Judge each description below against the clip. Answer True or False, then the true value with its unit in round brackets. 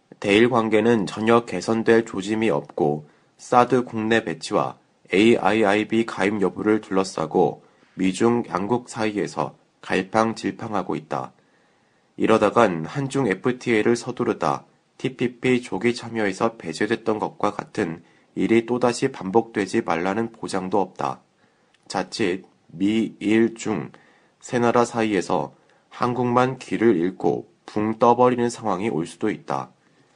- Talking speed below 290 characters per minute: True (260 characters per minute)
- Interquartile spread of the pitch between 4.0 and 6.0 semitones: False (2.9 semitones)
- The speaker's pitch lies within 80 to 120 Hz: True (115 Hz)